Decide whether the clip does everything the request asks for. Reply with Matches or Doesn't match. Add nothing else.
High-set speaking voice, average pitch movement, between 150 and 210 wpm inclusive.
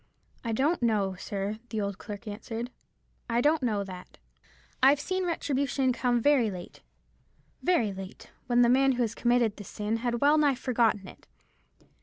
Matches